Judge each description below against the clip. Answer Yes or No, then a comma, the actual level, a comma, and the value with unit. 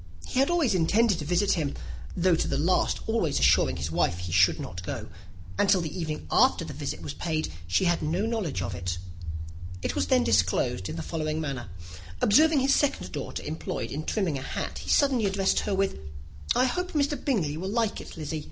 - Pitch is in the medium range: Yes, medium, 170 Hz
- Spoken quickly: Yes, fast, 210 wpm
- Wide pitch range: Yes, wide, 7.8 semitones